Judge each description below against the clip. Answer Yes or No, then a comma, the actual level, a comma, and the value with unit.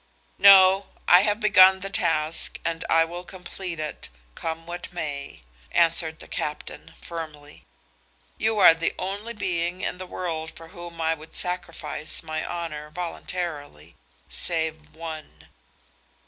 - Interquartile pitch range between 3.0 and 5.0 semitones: No, narrow, 2.5 semitones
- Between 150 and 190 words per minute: No, slow, 135 wpm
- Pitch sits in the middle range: Yes, medium, 170 Hz